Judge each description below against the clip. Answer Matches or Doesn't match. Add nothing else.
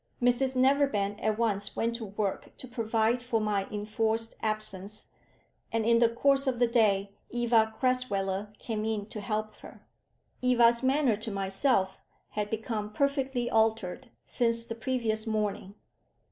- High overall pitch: Matches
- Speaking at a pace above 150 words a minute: Doesn't match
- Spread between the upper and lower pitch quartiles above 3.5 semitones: Doesn't match